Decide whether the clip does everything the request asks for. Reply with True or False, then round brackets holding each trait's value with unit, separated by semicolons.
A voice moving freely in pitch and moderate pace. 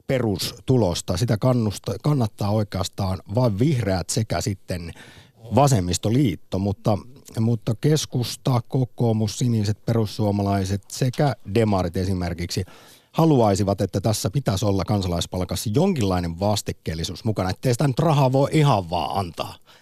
False (4.7 semitones; 110 wpm)